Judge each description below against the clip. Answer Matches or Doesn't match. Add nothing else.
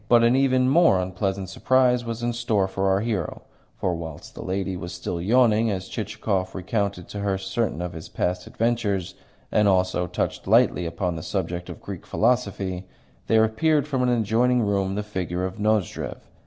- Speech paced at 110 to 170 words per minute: Doesn't match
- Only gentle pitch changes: Doesn't match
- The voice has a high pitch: Doesn't match